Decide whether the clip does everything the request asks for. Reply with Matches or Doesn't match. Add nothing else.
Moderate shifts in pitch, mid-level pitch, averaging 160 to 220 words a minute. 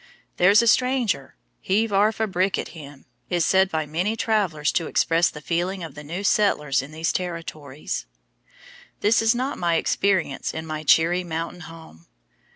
Matches